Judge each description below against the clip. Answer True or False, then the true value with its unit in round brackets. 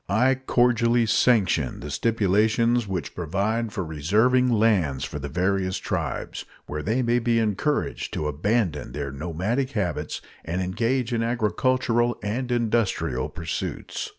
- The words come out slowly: True (130 wpm)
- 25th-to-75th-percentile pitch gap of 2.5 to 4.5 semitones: False (5.2 semitones)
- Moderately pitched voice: False (110 Hz)